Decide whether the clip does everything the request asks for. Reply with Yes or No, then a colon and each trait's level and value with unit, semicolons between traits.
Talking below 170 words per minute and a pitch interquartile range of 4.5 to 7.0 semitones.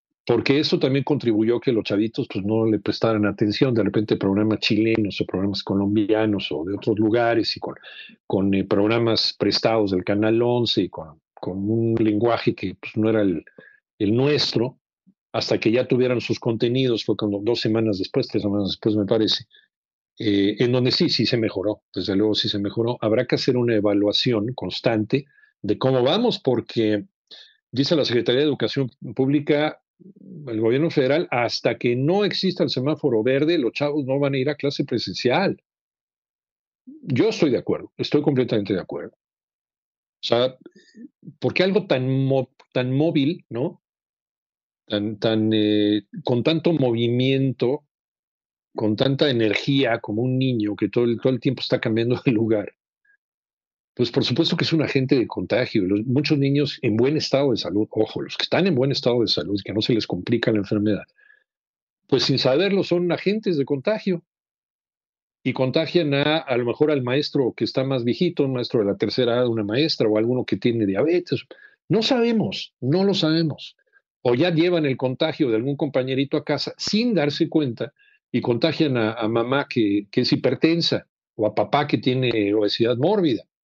No: average, 175 wpm; average, 5.3 semitones